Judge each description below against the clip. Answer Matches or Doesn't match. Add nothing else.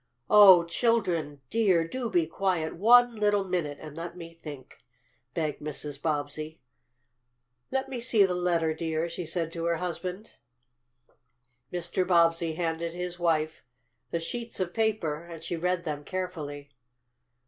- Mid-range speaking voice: Matches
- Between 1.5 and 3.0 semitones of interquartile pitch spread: Matches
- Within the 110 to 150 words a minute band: Matches